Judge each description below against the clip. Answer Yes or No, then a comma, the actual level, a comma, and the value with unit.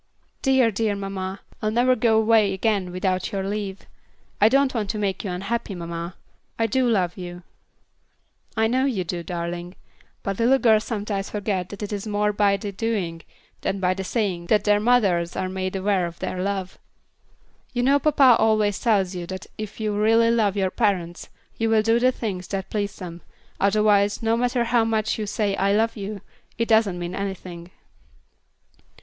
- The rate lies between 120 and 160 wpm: No, average, 180 wpm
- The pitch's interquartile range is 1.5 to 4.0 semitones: Yes, average, 3.1 semitones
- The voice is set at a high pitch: Yes, high, 205 Hz